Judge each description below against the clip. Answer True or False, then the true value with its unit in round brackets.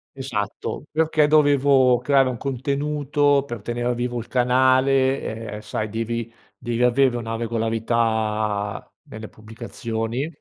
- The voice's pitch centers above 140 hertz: False (120 Hz)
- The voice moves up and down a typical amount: True (3.3 semitones)